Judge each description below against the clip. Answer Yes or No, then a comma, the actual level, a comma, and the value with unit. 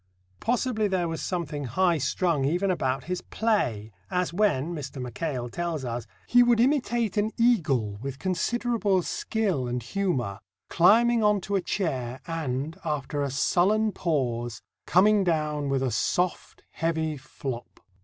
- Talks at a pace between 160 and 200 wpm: No, average, 145 wpm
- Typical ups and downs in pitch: No, wide, 7.2 semitones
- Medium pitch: Yes, medium, 165 Hz